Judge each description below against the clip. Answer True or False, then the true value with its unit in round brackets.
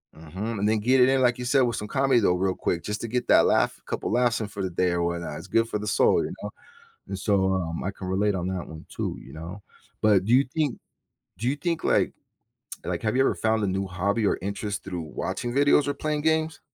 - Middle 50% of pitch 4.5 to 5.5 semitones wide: True (4.9 semitones)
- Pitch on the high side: False (105 Hz)